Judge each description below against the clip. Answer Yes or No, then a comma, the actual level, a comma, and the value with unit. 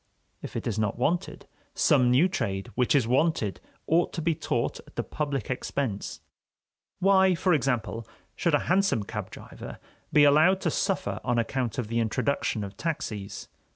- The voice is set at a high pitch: No, low, 130 Hz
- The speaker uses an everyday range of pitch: No, wide, 6.6 semitones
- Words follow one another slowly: No, average, 165 wpm